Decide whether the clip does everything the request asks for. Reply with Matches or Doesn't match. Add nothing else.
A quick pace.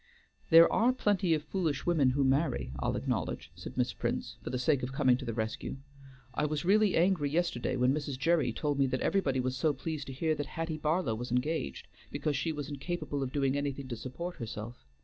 Matches